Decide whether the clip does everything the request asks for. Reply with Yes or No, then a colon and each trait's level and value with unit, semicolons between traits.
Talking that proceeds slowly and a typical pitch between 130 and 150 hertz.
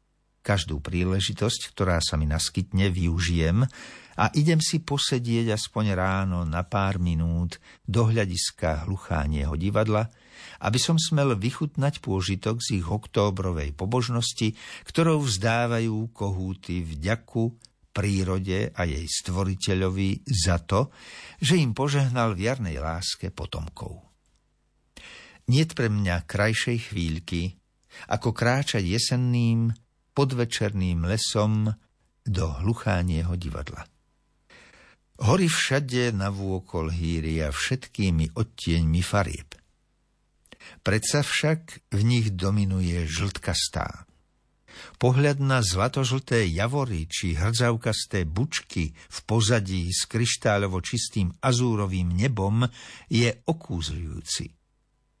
No: slow, 95 wpm; low, 100 Hz